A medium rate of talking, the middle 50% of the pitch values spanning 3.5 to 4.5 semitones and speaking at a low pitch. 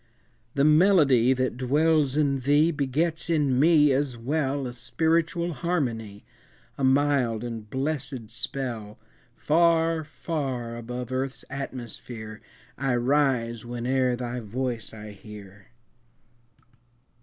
No: slow, 110 wpm; average, 4.0 semitones; low, 130 Hz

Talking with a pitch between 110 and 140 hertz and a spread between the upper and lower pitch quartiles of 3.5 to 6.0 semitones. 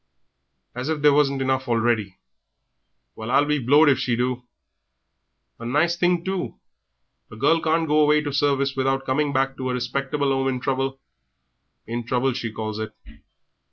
No: low, 135 Hz; average, 3.0 semitones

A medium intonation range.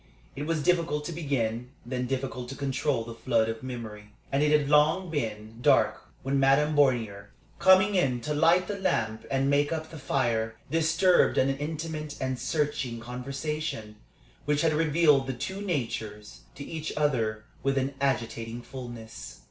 Yes: average, 4.5 semitones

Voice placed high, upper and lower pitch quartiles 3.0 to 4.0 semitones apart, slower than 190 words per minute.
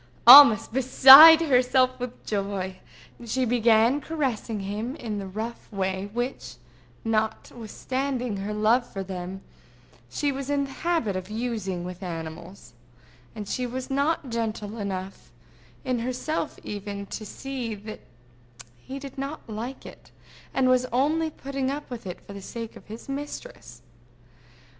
No: high, 235 Hz; average, 4.8 semitones; average, 145 wpm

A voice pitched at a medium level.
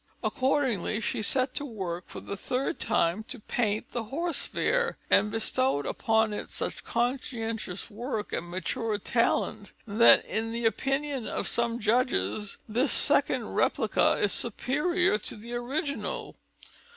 No: high, 230 Hz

